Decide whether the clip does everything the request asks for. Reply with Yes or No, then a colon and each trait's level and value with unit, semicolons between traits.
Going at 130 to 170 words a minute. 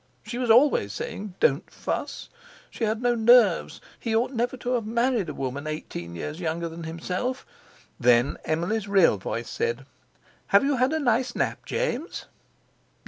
Yes: average, 160 wpm